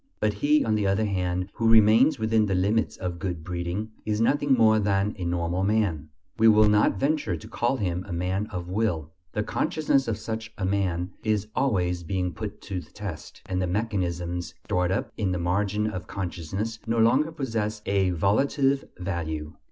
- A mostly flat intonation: No, average, 3.7 semitones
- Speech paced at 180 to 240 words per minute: Yes, average, 185 wpm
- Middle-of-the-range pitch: No, low, 100 Hz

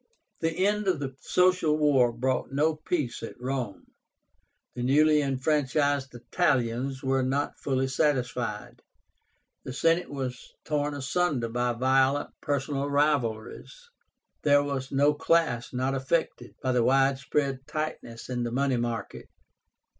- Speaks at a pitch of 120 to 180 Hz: Yes, low, 135 Hz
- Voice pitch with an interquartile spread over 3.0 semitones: No, average, 2.7 semitones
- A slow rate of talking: Yes, slow, 130 wpm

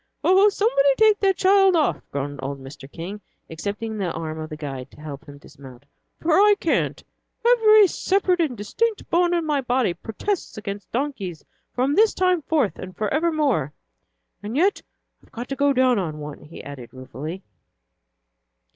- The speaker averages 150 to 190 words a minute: Yes, average, 165 wpm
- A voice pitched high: Yes, high, 245 Hz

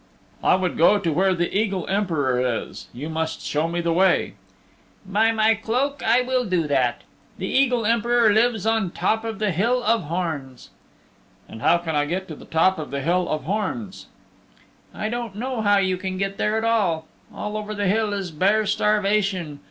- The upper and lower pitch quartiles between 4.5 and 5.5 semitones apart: Yes, average, 4.8 semitones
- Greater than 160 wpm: Yes, average, 195 wpm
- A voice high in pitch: Yes, high, 195 Hz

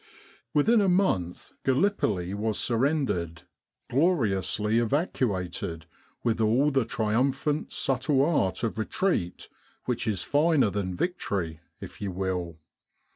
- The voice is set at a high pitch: No, low, 115 Hz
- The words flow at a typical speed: No, slow, 110 wpm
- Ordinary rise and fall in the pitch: No, wide, 7.3 semitones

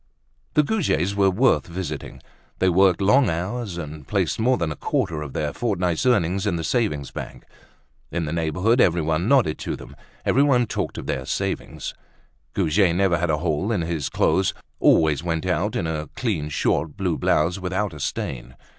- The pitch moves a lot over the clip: No, average, 4.7 semitones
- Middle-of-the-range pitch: No, very low, 85 Hz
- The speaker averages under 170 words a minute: No, average, 175 wpm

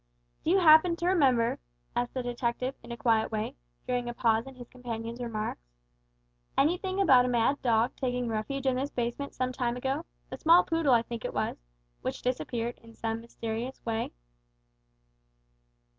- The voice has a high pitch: Yes, high, 245 Hz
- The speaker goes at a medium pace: Yes, average, 170 wpm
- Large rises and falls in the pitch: No, average, 2.8 semitones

